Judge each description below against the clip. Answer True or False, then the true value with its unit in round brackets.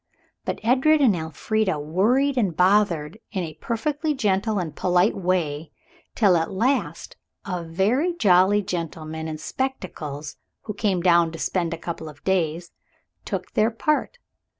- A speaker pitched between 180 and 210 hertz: True (185 Hz)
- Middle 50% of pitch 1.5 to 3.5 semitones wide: False (5.3 semitones)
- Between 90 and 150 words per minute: True (145 wpm)